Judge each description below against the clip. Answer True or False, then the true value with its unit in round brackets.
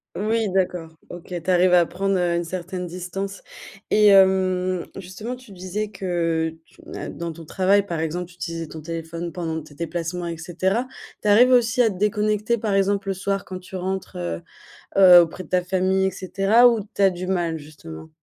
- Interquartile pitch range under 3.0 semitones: True (2.6 semitones)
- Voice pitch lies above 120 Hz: True (185 Hz)